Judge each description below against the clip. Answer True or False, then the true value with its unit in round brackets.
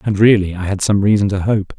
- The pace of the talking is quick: True (270 wpm)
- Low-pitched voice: True (100 Hz)